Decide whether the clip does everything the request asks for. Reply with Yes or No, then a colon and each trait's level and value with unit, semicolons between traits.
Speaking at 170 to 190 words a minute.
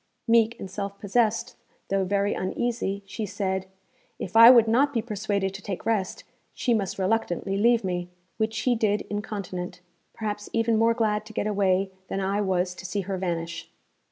Yes: average, 175 wpm